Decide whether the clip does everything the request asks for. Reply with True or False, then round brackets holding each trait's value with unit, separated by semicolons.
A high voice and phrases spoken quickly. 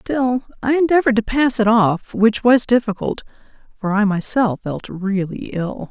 False (225 Hz; 165 wpm)